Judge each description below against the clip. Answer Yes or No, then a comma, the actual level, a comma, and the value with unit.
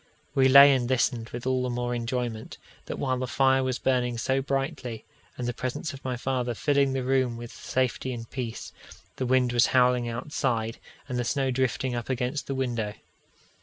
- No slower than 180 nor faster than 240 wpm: Yes, average, 190 wpm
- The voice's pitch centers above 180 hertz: No, low, 125 Hz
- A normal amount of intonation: No, narrow, 1.6 semitones